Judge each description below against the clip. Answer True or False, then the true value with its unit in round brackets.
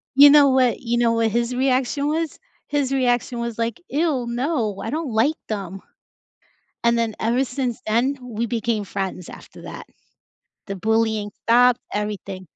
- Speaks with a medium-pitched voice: False (235 Hz)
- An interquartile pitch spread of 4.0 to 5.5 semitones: False (3.2 semitones)